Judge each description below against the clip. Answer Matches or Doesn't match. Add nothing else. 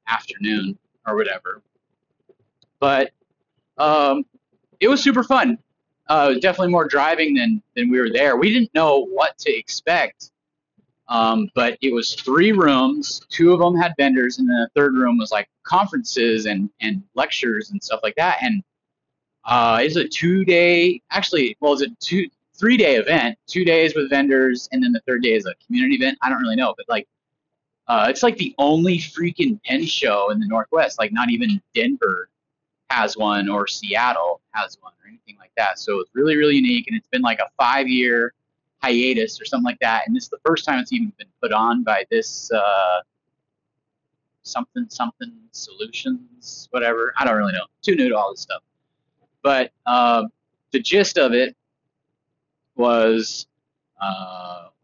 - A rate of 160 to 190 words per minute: Matches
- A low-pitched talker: Doesn't match